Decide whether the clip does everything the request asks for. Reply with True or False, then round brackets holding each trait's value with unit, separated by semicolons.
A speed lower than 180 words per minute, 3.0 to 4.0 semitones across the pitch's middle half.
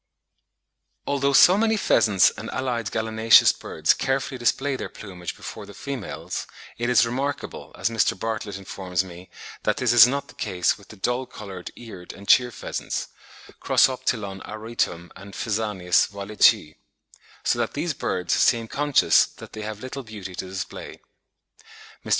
False (150 wpm; 4.6 semitones)